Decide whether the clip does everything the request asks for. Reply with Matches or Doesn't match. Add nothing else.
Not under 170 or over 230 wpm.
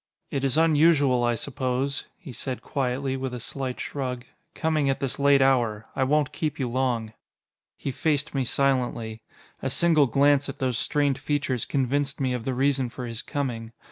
Matches